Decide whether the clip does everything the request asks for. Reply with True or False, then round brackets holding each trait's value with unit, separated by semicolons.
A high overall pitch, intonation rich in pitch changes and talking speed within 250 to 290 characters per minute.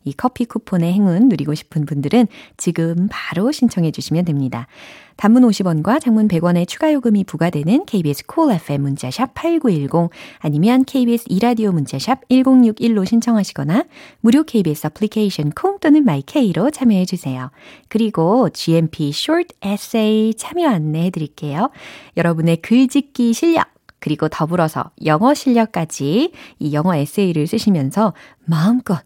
False (205 Hz; 7.8 semitones; 340 characters per minute)